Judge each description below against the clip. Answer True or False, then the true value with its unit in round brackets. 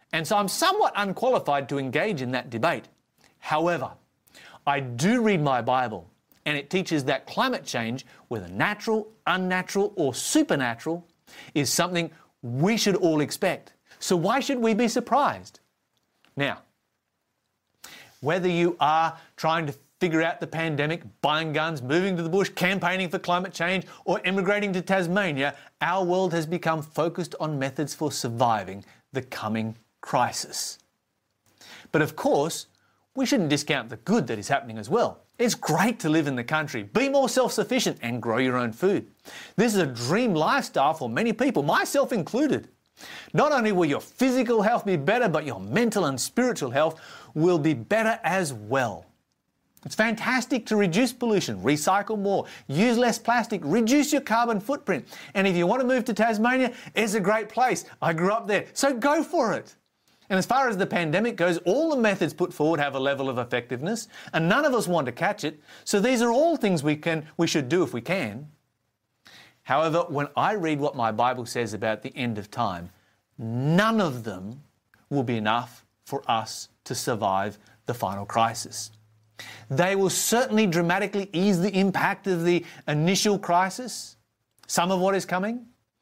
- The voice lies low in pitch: False (175 Hz)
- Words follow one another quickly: False (170 wpm)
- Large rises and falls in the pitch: True (7.4 semitones)